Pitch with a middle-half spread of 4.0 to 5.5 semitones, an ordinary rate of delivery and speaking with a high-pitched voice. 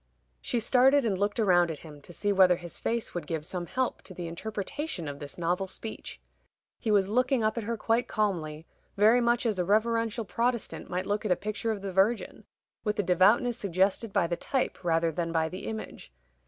No: average, 4.6 semitones; fast, 210 wpm; high, 200 Hz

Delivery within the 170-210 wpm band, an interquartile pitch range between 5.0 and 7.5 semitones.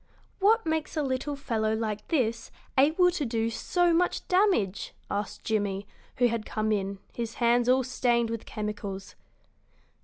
No: average, 150 wpm; average, 5.3 semitones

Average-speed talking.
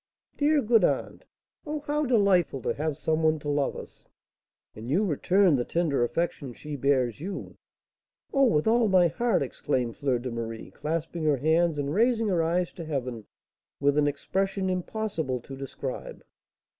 Yes: average, 165 wpm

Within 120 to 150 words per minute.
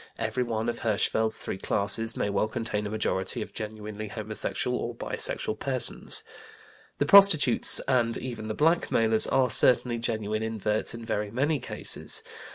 Yes: average, 145 wpm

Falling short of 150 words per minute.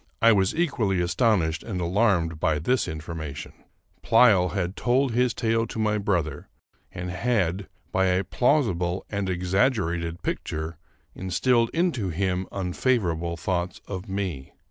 Yes: slow, 135 wpm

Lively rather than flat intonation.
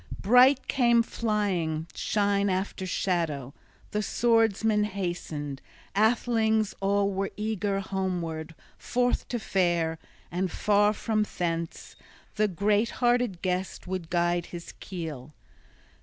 No: average, 3.9 semitones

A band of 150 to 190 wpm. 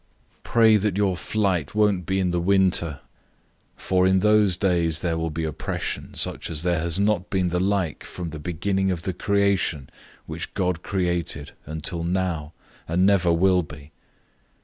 Yes: average, 170 wpm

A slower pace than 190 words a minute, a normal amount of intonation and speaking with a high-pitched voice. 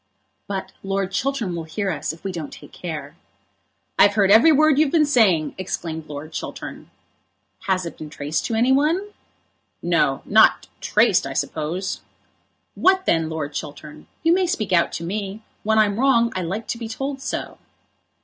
No: average, 170 wpm; wide, 8.0 semitones; high, 195 Hz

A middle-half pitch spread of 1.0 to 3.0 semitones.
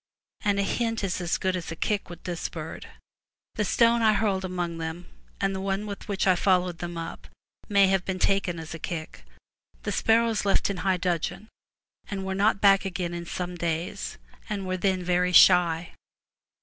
Yes: narrow, 2.4 semitones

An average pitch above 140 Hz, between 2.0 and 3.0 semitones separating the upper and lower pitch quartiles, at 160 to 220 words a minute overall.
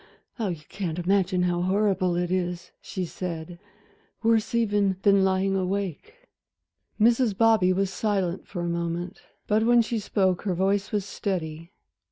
No: high, 190 Hz; average, 2.7 semitones; average, 150 wpm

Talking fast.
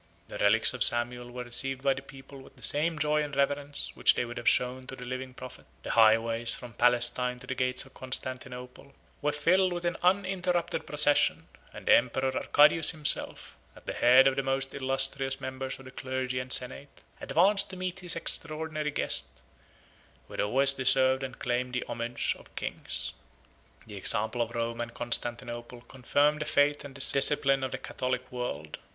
No: average, 185 wpm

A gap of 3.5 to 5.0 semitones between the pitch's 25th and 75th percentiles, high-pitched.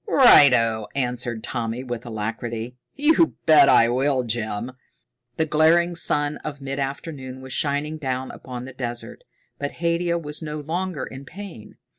No: average, 4.5 semitones; low, 135 Hz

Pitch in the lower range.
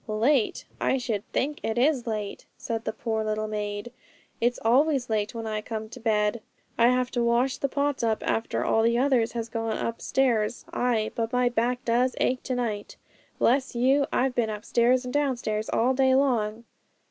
No: high, 235 Hz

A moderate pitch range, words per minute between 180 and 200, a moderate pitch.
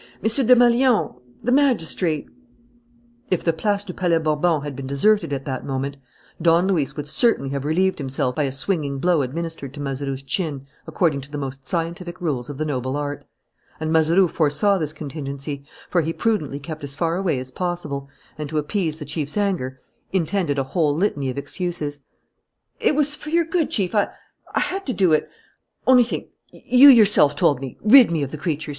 No: wide, 5.8 semitones; average, 190 wpm; medium, 160 Hz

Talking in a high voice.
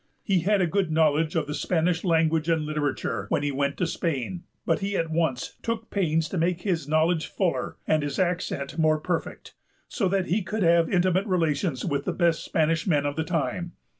No: medium, 165 Hz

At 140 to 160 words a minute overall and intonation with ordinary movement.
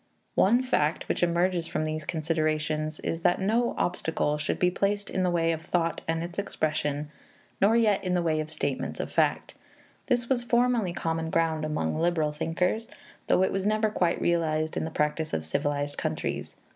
No: average, 185 wpm; average, 3.5 semitones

